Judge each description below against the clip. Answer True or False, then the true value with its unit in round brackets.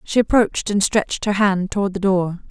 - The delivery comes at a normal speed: False (215 wpm)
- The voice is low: False (200 Hz)